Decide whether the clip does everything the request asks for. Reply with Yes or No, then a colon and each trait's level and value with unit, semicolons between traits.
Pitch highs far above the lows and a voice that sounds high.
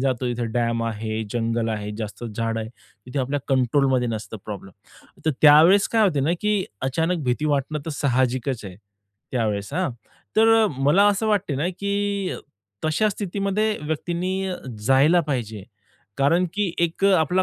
No: wide, 8.0 semitones; medium, 145 Hz